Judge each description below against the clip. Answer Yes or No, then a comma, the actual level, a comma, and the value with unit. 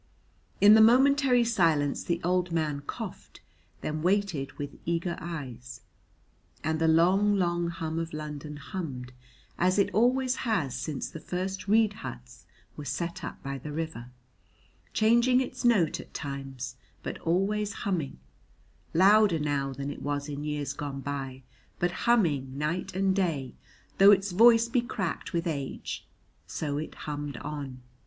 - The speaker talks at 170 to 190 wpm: No, average, 150 wpm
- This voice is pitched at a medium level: Yes, medium, 165 Hz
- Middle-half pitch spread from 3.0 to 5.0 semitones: No, wide, 5.6 semitones